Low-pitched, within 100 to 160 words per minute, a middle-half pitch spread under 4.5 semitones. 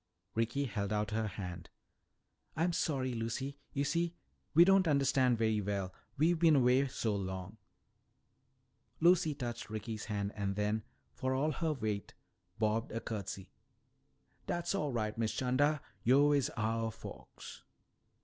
No: low, 120 Hz; average, 140 wpm; average, 5.2 semitones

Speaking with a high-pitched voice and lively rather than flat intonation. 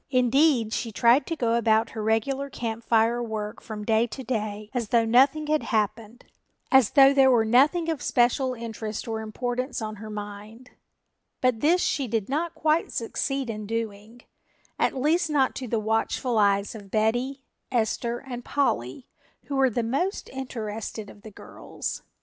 No: high, 235 Hz; average, 3.4 semitones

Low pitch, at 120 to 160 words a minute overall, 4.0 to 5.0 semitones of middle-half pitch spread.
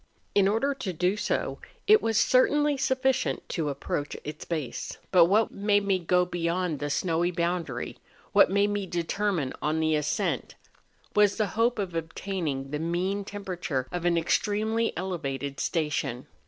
No: medium, 180 Hz; average, 145 wpm; average, 4.5 semitones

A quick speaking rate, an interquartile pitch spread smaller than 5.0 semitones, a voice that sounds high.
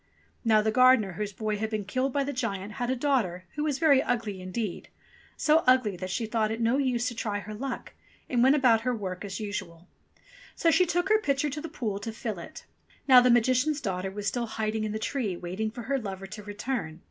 Yes: fast, 230 wpm; average, 4.2 semitones; high, 225 Hz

